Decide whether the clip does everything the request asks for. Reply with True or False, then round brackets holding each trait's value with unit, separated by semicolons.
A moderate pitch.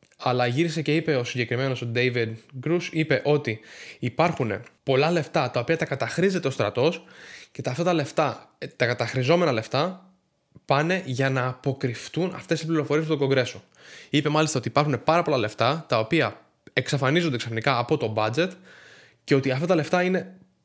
True (145 Hz)